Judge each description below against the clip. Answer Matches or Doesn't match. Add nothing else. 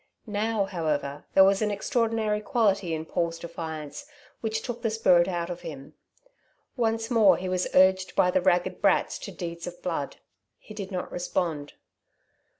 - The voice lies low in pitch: Doesn't match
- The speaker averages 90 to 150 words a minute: Doesn't match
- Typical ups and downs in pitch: Matches